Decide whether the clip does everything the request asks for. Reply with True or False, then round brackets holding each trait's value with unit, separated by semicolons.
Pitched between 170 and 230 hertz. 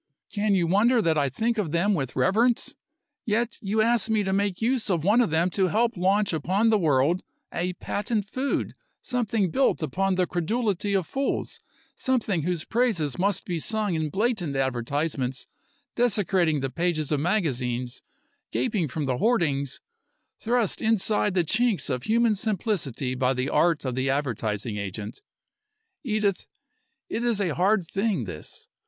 True (185 Hz)